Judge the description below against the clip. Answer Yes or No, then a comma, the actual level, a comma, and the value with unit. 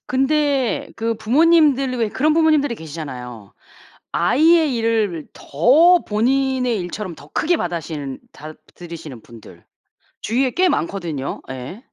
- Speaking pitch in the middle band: No, high, 225 Hz